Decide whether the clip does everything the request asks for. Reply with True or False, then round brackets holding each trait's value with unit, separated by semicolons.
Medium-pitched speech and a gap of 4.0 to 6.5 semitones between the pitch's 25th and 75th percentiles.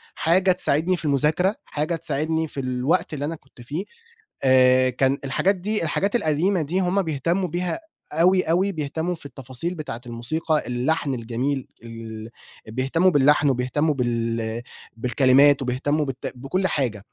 True (145 Hz; 4.7 semitones)